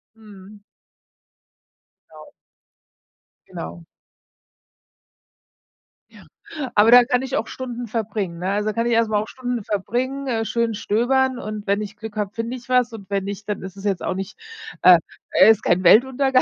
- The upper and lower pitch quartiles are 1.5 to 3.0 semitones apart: No, average, 3.4 semitones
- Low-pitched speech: No, high, 220 Hz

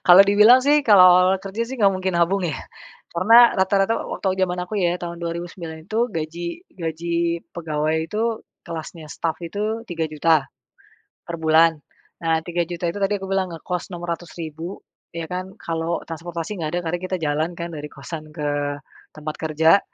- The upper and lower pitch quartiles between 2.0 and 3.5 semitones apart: Yes, average, 2.8 semitones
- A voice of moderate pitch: Yes, medium, 170 Hz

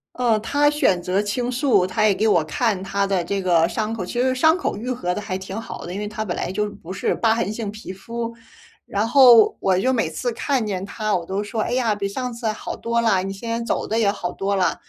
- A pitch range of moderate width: Yes, average, 3.3 semitones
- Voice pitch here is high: Yes, high, 210 Hz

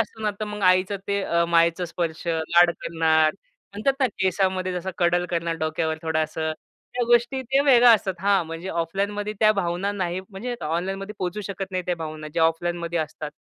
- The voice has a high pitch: No, medium, 180 Hz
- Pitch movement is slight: No, average, 3.4 semitones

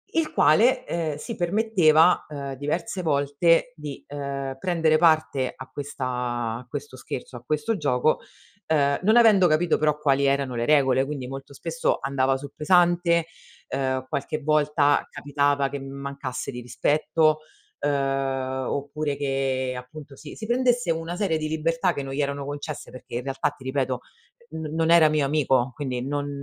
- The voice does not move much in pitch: No, average, 3.0 semitones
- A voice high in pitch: No, medium, 145 Hz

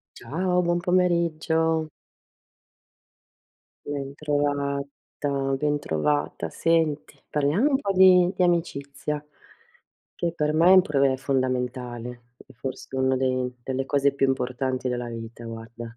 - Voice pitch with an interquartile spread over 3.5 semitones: Yes, average, 4.1 semitones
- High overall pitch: No, medium, 140 Hz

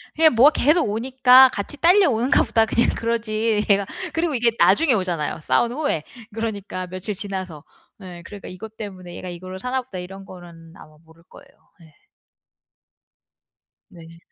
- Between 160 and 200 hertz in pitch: No, high, 210 Hz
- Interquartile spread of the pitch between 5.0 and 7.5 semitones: Yes, wide, 5.4 semitones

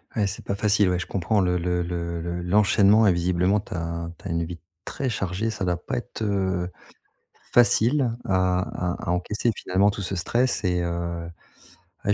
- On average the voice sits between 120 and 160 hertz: No, very low, 95 Hz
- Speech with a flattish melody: No, average, 3.0 semitones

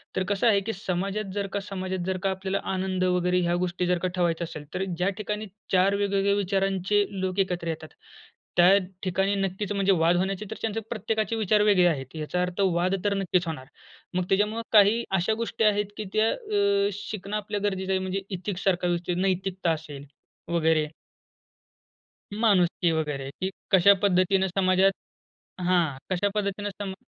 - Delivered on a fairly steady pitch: Yes, narrow, 2.1 semitones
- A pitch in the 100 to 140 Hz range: No, high, 190 Hz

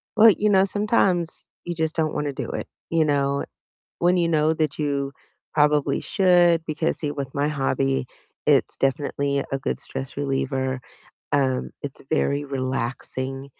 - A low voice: No, medium, 145 Hz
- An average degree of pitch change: Yes, average, 3.1 semitones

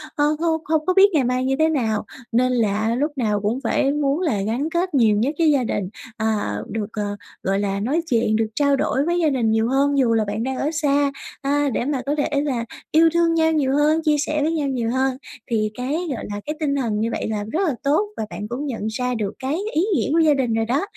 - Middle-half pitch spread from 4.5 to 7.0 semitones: Yes, average, 5.2 semitones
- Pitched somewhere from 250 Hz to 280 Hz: Yes, very high, 270 Hz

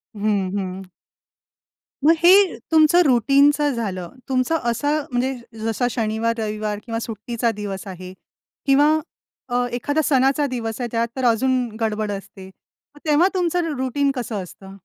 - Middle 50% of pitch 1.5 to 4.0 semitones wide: No, average, 4.9 semitones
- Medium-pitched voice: No, high, 235 Hz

